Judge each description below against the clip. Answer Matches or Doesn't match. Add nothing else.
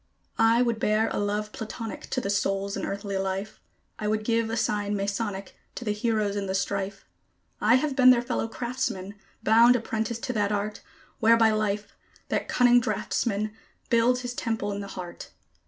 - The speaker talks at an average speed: Matches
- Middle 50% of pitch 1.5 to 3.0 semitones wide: Matches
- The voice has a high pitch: Matches